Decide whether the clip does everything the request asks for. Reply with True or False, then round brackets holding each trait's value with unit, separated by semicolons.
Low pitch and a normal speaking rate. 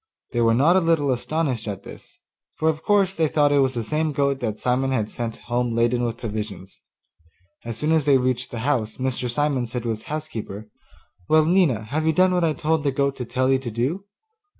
False (130 Hz; 220 wpm)